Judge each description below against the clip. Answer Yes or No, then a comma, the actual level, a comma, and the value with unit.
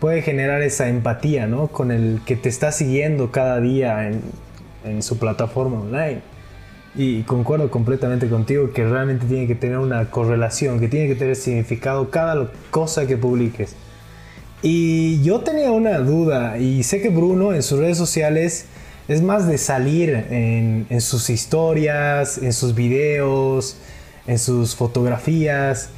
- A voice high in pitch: No, low, 130 Hz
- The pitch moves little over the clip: No, average, 4.1 semitones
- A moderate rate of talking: Yes, average, 150 wpm